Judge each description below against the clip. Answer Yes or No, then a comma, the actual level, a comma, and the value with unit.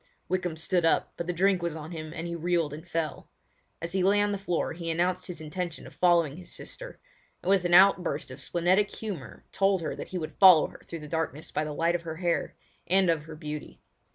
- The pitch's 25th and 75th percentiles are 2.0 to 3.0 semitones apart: Yes, narrow, 2.5 semitones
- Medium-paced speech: No, fast, 235 wpm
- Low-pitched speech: No, medium, 170 Hz